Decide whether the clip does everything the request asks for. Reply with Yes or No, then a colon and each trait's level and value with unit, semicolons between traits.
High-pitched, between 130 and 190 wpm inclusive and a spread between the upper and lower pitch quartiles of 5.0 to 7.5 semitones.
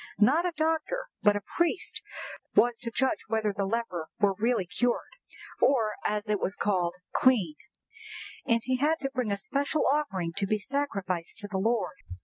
Yes: high, 225 Hz; average, 170 wpm; average, 5.3 semitones